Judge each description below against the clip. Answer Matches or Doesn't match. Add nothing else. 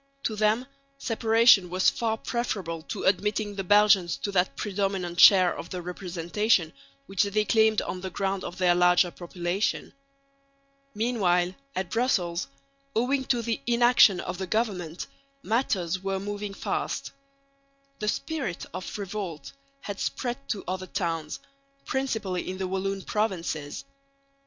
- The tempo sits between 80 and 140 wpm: Matches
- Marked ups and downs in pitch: Doesn't match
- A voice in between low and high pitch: Doesn't match